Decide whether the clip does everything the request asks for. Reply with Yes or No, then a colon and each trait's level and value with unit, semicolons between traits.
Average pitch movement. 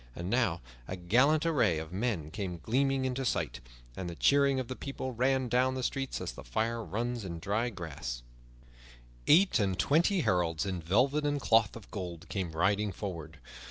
No: wide, 6.8 semitones